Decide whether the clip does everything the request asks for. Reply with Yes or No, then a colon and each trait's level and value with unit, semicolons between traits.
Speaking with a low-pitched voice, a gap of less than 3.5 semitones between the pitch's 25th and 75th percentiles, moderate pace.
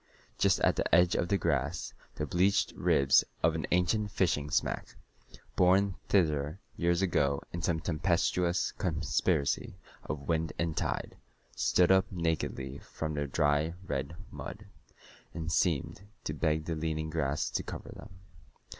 Yes: very low, 80 Hz; average, 3.0 semitones; average, 145 wpm